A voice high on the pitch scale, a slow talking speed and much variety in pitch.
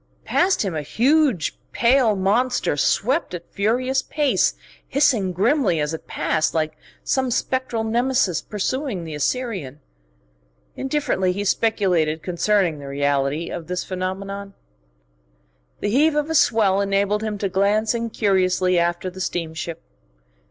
Yes: high, 200 Hz; slow, 130 wpm; wide, 5.9 semitones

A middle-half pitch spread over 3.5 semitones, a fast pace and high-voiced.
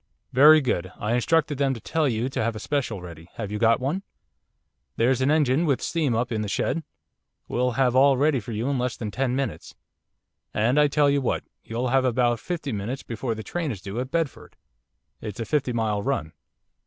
No: average, 3.9 semitones; fast, 210 wpm; low, 125 Hz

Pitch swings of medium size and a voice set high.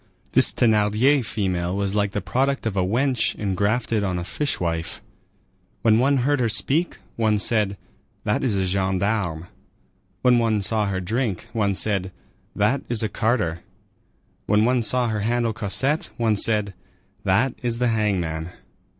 No: average, 3.6 semitones; low, 105 Hz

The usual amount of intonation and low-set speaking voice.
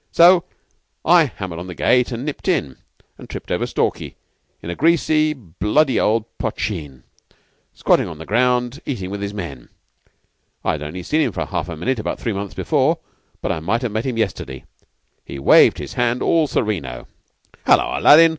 No: wide, 7.5 semitones; low, 110 Hz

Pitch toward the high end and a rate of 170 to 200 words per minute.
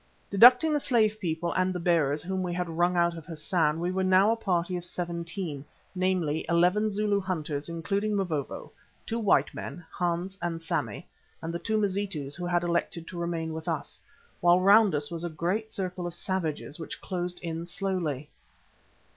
No: medium, 175 Hz; average, 180 wpm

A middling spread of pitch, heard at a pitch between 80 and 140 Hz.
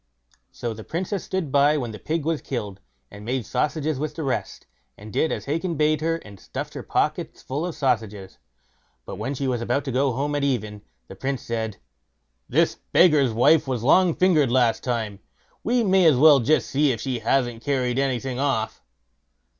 Yes: average, 4.6 semitones; low, 135 Hz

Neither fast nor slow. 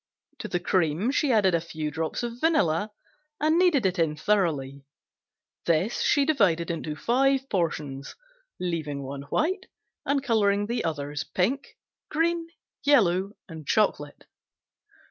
No: slow, 130 wpm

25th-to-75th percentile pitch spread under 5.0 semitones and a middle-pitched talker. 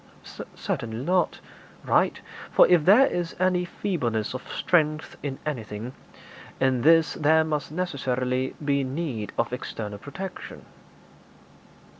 No: wide, 5.4 semitones; medium, 145 Hz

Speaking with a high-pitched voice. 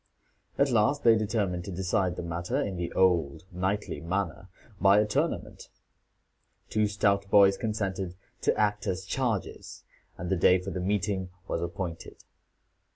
No: very low, 95 Hz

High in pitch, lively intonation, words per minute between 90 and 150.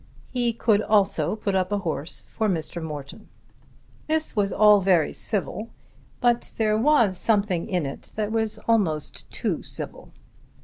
No: high, 210 Hz; average, 3.6 semitones; average, 145 wpm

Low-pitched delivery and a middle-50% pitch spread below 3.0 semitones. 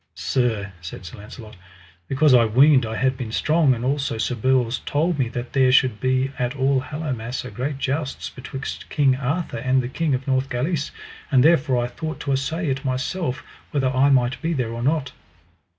Yes: low, 130 Hz; narrow, 2.5 semitones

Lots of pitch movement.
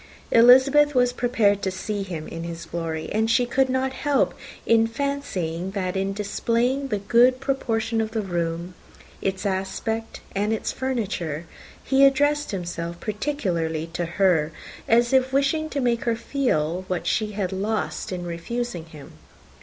Yes: wide, 6.2 semitones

